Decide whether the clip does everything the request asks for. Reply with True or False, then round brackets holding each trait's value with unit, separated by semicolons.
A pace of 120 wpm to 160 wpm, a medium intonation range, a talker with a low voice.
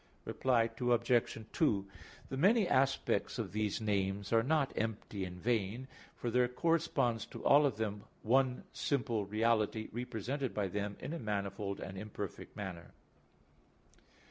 True (140 wpm; 4.2 semitones; 115 Hz)